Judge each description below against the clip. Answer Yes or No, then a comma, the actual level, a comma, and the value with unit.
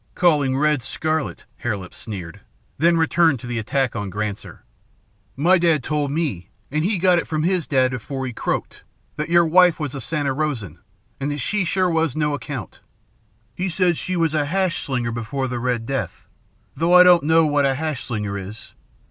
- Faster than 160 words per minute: Yes, average, 190 wpm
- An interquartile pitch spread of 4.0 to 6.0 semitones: Yes, average, 5.1 semitones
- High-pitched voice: No, medium, 145 Hz